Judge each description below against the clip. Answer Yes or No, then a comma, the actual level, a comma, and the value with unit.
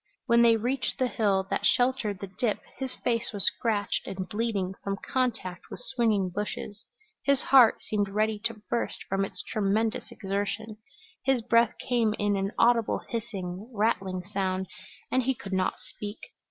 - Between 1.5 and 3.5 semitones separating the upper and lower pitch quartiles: Yes, average, 3.2 semitones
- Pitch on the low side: No, high, 215 Hz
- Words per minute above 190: No, average, 160 wpm